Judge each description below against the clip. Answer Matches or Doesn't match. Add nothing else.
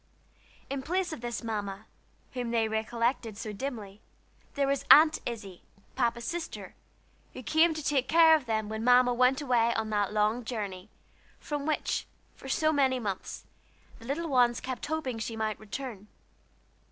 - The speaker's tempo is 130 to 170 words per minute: Matches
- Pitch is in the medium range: Doesn't match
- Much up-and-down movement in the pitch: Doesn't match